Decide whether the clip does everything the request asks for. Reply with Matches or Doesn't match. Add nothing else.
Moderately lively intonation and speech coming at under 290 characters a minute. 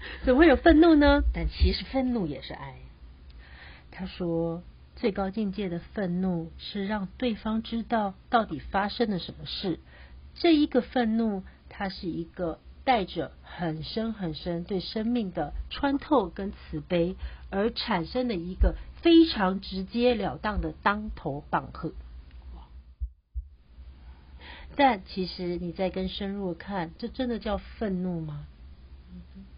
Doesn't match